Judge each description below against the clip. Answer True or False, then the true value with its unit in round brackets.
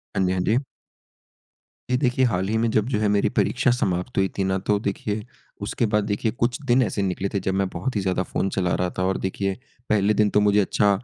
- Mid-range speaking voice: False (100 Hz)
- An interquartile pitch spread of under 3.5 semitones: True (2.4 semitones)